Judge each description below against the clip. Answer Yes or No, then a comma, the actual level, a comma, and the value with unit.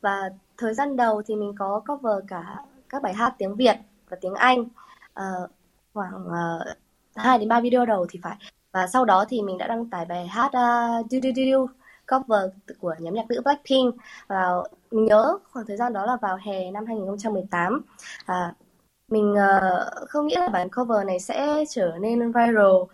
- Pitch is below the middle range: No, high, 215 Hz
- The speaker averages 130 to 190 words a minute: Yes, average, 185 wpm